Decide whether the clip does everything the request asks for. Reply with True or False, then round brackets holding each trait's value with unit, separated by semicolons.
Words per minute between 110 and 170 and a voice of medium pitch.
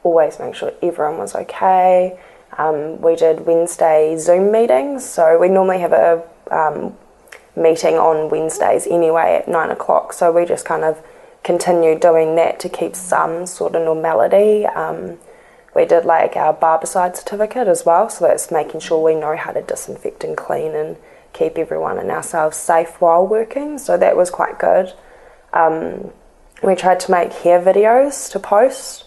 True (165 wpm; 175 Hz)